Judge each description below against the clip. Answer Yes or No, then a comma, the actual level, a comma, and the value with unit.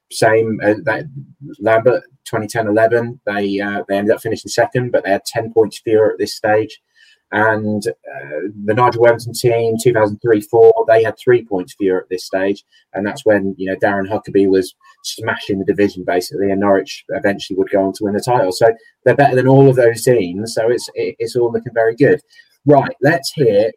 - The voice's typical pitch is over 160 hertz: No, low, 115 Hz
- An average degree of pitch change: Yes, average, 4.7 semitones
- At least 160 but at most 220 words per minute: Yes, average, 190 wpm